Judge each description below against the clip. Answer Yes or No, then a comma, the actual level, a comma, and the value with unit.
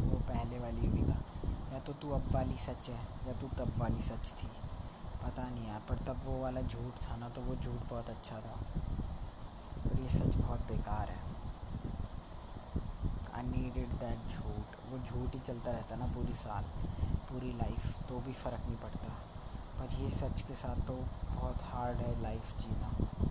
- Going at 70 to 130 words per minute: No, average, 180 wpm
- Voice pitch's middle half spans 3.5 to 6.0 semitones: No, average, 3.0 semitones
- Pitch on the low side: Yes, low, 120 Hz